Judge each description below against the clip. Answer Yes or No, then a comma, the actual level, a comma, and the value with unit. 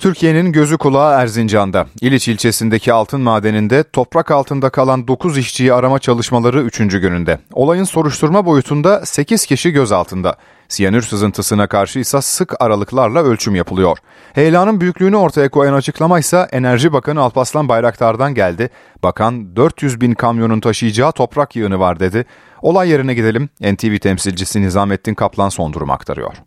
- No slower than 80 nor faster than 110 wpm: No, fast, 140 wpm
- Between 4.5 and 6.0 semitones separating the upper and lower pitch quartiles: Yes, wide, 5.5 semitones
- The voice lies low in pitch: Yes, low, 125 Hz